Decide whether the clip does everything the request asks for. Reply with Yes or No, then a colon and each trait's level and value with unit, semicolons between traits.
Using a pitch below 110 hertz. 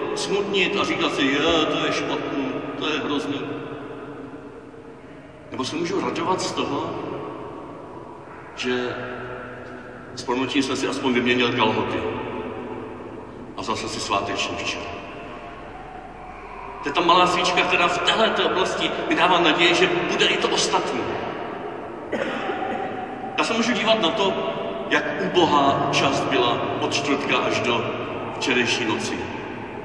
No: medium, 140 Hz